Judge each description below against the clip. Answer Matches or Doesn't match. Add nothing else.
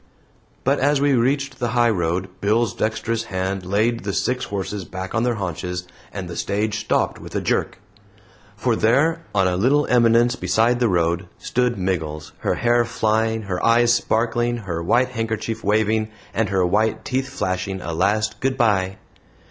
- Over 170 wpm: Doesn't match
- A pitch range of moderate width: Matches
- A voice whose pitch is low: Matches